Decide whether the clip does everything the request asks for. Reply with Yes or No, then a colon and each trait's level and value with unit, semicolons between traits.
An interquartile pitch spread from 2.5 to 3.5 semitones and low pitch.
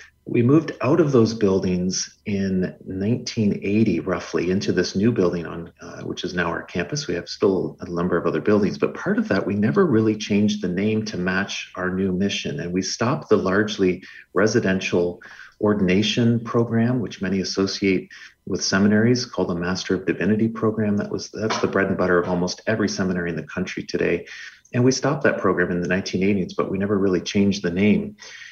Yes: average, 3.2 semitones; very low, 95 Hz